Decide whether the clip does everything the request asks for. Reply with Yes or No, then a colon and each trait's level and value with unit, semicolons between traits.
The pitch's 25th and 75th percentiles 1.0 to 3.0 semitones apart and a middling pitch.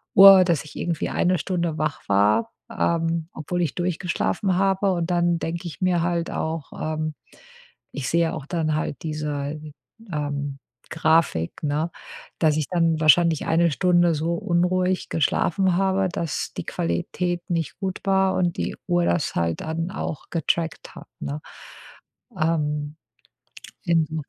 Yes: narrow, 2.4 semitones; medium, 165 Hz